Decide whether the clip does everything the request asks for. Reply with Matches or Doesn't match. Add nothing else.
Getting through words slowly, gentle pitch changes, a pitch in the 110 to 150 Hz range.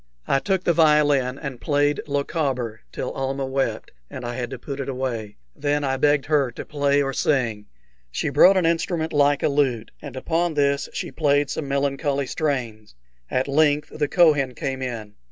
Doesn't match